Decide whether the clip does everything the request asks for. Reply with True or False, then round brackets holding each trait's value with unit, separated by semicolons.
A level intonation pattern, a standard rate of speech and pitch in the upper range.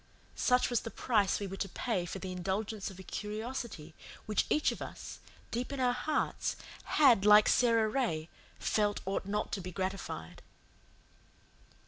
False (3.9 semitones; 160 wpm; 210 Hz)